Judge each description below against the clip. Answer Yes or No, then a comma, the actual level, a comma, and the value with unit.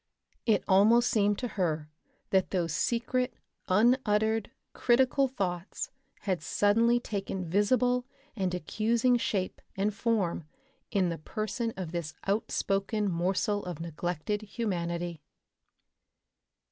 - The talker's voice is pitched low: No, high, 205 Hz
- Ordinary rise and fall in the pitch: Yes, average, 4.5 semitones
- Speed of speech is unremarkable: No, slow, 110 wpm